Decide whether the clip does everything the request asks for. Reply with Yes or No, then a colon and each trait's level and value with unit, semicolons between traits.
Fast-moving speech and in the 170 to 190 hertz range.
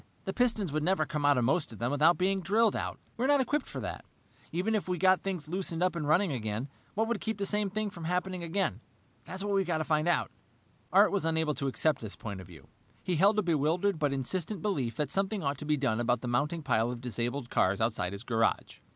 No: fast, 245 wpm; medium, 160 Hz